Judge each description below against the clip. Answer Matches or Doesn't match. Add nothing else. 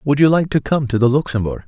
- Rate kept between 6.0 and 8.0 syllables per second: Matches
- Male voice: Matches